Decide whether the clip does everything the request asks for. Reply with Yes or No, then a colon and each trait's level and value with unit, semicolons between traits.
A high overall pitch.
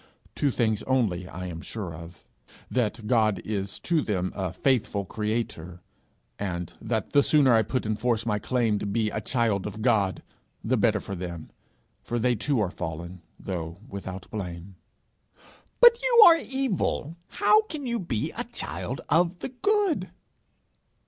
No: low, 110 Hz